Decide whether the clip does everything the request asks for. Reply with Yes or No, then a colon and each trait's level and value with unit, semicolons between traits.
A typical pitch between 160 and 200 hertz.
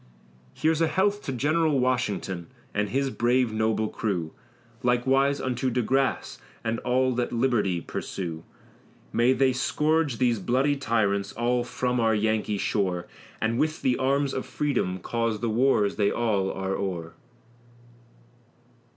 No: low, 120 Hz